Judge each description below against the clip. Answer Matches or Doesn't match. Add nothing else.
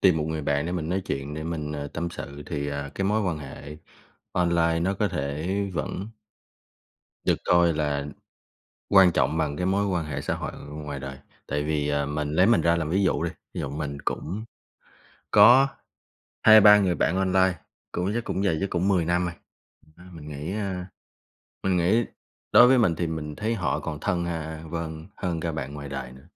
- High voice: Doesn't match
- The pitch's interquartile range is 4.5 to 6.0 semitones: Doesn't match